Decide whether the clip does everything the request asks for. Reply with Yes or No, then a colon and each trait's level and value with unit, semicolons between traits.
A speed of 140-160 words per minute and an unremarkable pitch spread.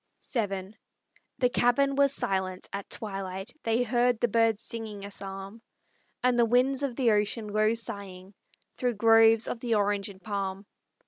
Yes: average, 155 wpm; average, 3.3 semitones